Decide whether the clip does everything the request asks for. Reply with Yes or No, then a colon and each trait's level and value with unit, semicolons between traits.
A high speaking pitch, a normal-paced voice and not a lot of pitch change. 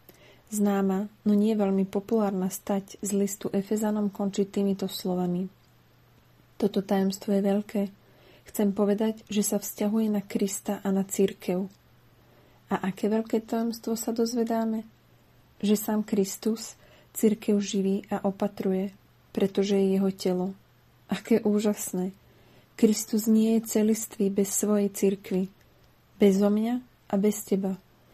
Yes: high, 205 Hz; average, 125 wpm; narrow, 1.8 semitones